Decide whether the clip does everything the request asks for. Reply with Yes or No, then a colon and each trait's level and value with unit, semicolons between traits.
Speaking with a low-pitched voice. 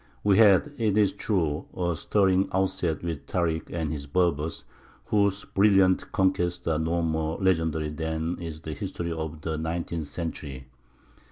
Yes: very low, 85 Hz